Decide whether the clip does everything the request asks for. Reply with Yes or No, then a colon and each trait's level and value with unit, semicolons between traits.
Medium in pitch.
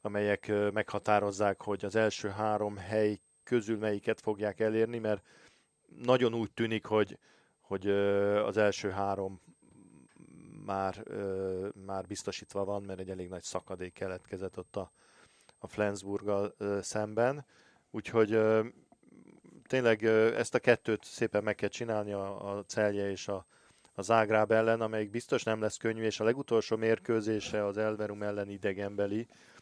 No: low, 105 Hz